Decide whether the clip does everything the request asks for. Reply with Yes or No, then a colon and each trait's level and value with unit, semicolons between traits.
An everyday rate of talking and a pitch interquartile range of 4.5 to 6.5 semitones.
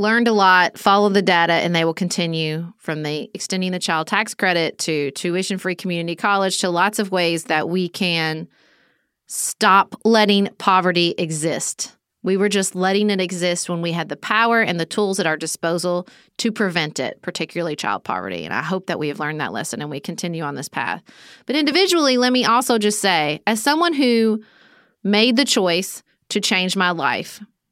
No: average, 190 wpm; average, 3.9 semitones